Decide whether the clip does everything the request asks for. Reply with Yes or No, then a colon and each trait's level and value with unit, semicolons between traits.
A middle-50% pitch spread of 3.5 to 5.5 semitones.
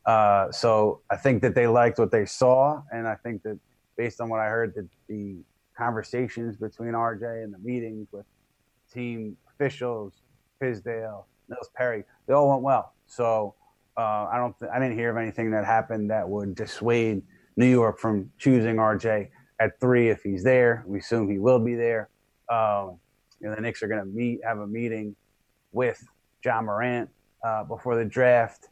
No: narrow, 2.4 semitones